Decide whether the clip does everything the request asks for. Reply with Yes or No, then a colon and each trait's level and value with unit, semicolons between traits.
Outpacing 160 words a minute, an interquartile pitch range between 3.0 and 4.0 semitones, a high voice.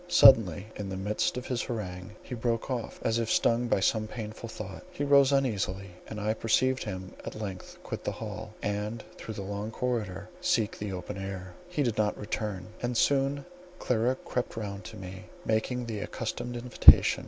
No: average, 185 wpm; average, 3.5 semitones; low, 110 Hz